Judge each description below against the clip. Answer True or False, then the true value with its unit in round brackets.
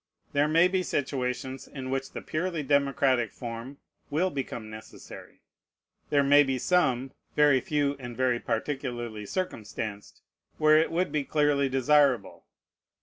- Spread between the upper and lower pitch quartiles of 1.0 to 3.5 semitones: True (3.0 semitones)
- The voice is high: False (135 Hz)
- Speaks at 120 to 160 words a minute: True (135 wpm)